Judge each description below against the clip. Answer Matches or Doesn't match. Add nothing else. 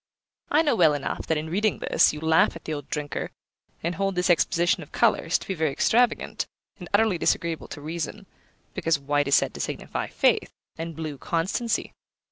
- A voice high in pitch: Doesn't match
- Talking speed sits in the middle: Matches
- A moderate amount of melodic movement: Matches